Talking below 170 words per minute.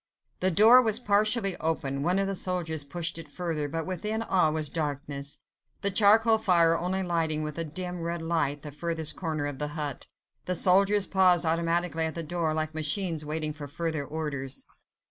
No: average, 185 wpm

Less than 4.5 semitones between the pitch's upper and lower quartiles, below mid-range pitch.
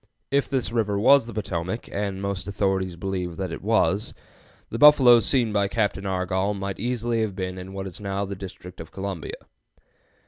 Yes: average, 3.0 semitones; low, 100 Hz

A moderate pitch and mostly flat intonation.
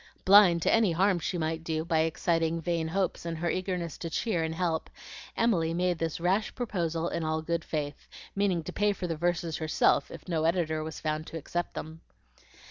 Yes: medium, 165 Hz; narrow, 2.0 semitones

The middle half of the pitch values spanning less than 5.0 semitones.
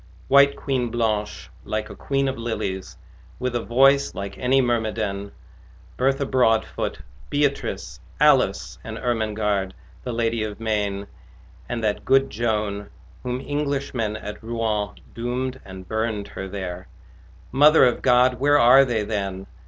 Yes: average, 3.8 semitones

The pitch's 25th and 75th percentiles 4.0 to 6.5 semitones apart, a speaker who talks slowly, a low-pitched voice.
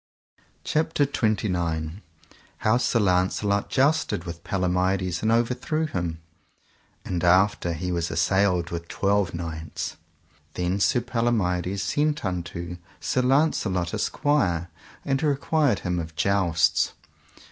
Yes: wide, 5.5 semitones; slow, 115 wpm; very low, 95 Hz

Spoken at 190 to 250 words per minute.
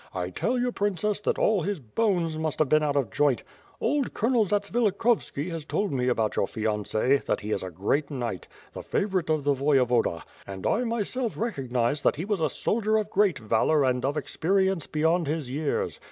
Yes: average, 195 wpm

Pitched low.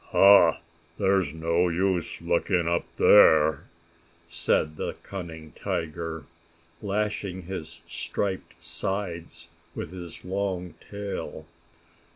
Yes: very low, 85 Hz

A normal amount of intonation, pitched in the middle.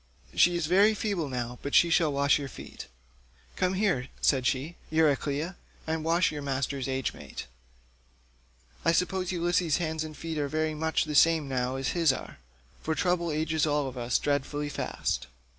Yes: average, 3.4 semitones; medium, 155 Hz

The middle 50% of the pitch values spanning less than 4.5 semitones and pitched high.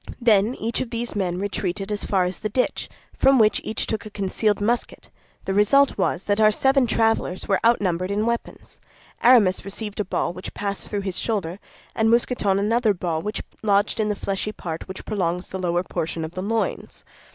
Yes: average, 3.0 semitones; high, 205 Hz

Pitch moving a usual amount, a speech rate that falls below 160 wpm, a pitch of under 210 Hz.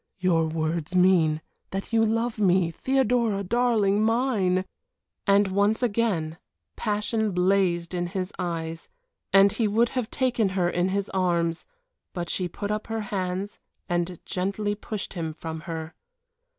Yes: average, 3.6 semitones; average, 140 wpm; high, 190 Hz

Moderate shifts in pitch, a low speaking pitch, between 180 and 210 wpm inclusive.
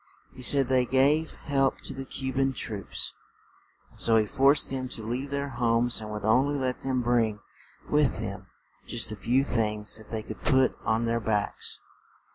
Yes: average, 3.3 semitones; low, 125 Hz; average, 190 wpm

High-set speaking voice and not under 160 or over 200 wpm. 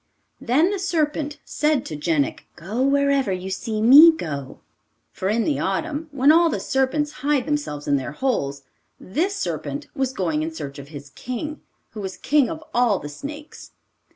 Yes: very high, 255 Hz; average, 175 wpm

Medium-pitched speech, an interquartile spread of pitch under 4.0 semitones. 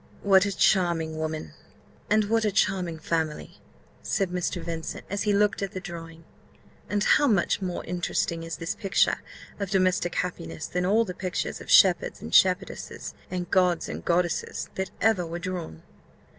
Yes: medium, 180 Hz; average, 2.8 semitones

